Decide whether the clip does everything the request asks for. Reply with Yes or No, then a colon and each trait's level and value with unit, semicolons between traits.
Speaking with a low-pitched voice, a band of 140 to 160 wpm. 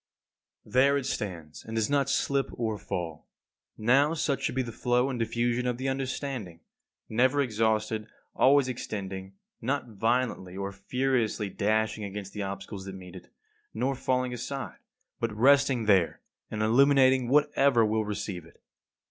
Yes: low, 115 Hz; average, 150 wpm